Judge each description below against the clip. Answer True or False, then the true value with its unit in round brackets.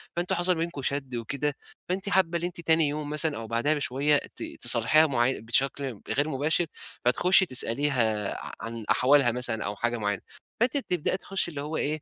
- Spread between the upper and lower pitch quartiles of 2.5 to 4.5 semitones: False (5.1 semitones)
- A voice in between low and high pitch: True (145 Hz)